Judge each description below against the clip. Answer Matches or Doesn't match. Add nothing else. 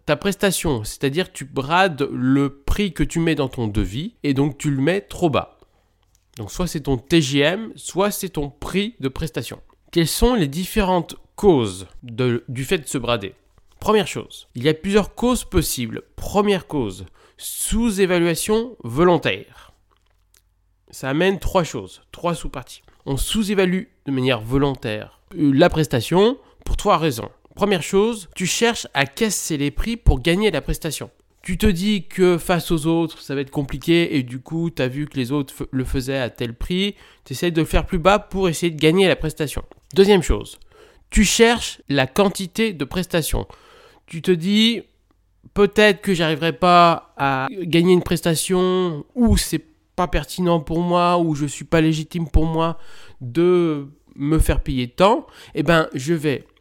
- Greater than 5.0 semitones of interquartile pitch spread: Matches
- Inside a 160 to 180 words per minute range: Matches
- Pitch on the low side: Doesn't match